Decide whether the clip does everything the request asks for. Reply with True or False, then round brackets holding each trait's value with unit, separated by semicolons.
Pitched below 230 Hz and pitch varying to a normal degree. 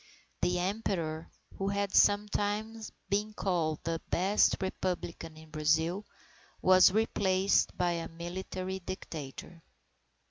True (185 Hz; 3.3 semitones)